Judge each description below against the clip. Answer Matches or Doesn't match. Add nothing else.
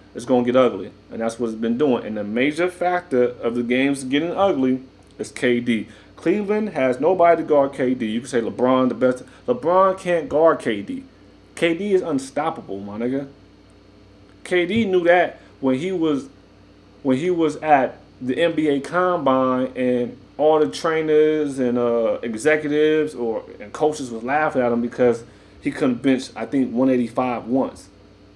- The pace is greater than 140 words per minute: Matches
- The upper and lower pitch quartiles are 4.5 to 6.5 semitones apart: Matches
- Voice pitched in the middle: Doesn't match